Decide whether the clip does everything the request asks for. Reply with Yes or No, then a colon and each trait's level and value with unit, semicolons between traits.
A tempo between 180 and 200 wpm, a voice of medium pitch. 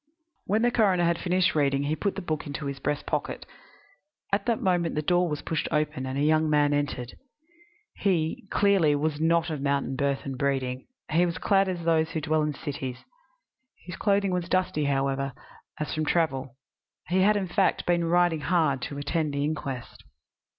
Yes: average, 185 wpm; medium, 155 Hz